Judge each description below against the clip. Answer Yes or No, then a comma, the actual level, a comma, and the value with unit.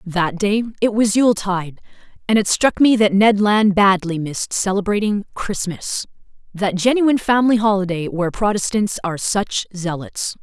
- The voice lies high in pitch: Yes, high, 200 Hz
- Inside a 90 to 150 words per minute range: Yes, average, 145 wpm